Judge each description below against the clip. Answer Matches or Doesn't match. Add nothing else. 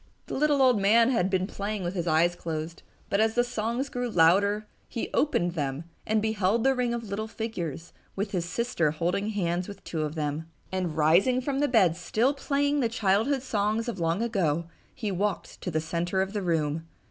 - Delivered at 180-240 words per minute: Matches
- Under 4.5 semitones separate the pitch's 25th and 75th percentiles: Doesn't match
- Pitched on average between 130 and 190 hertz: Doesn't match